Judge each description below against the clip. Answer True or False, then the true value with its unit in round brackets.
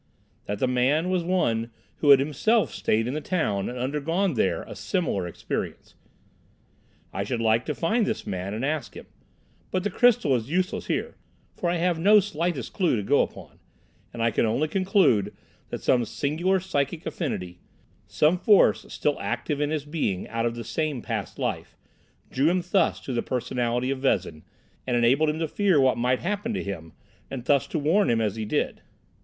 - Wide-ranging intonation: True (6.8 semitones)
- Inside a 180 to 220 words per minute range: True (190 wpm)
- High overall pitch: False (140 Hz)